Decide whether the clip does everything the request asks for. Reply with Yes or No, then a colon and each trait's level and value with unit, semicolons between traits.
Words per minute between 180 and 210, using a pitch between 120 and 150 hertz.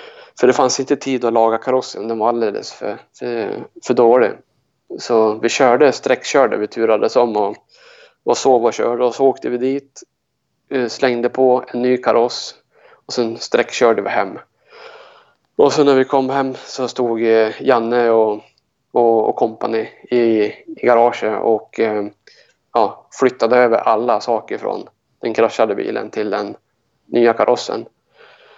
No: average, 150 wpm; low, 125 Hz